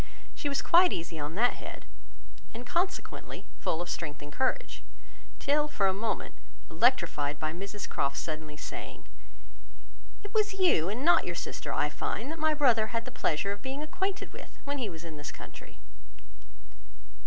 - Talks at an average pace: Yes, average, 170 wpm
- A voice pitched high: Yes, high, 230 Hz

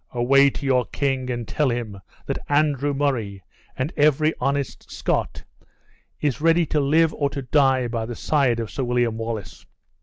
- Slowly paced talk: No, average, 170 wpm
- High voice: No, low, 135 Hz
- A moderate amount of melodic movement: Yes, average, 3.3 semitones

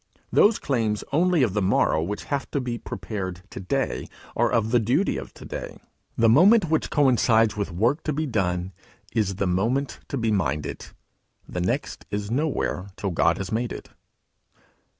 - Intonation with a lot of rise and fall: Yes, wide, 6.1 semitones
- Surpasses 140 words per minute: Yes, average, 175 wpm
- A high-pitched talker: No, low, 115 Hz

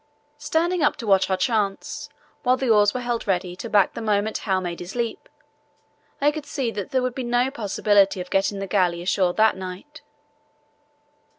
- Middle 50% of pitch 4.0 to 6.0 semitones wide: Yes, average, 4.7 semitones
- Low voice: No, high, 210 Hz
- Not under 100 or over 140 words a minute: No, average, 195 wpm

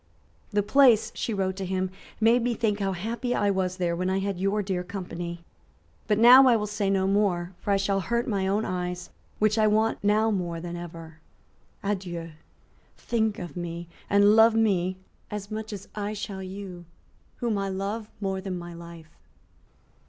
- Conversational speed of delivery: Yes, average, 180 wpm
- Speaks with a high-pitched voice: Yes, high, 195 Hz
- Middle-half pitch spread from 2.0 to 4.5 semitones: Yes, average, 3.0 semitones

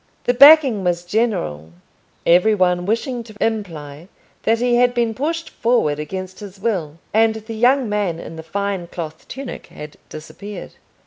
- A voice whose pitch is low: No, high, 205 Hz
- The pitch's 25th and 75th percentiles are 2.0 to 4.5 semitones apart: No, wide, 5.5 semitones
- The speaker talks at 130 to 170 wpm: Yes, average, 155 wpm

